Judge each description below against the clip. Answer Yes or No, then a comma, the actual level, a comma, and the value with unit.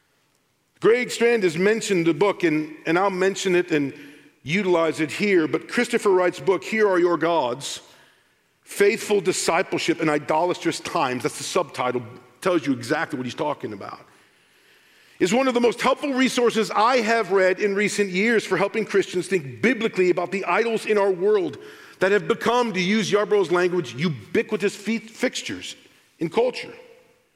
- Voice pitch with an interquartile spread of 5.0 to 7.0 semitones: Yes, average, 5.3 semitones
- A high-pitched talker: Yes, high, 195 Hz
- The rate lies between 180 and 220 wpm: No, average, 160 wpm